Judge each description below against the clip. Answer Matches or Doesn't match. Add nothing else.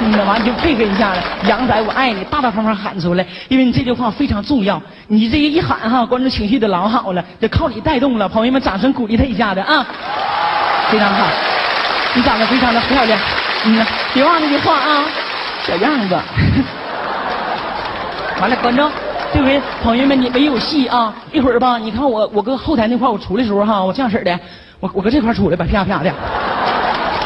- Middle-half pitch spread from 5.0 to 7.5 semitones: Doesn't match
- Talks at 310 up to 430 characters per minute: Doesn't match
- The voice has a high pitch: Matches